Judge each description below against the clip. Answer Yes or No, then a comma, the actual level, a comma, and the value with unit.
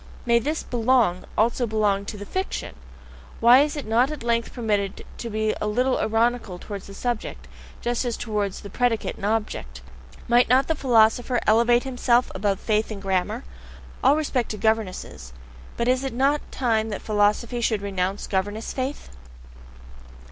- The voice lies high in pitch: Yes, high, 225 Hz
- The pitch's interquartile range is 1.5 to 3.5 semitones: Yes, average, 3.0 semitones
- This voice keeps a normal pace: Yes, average, 160 wpm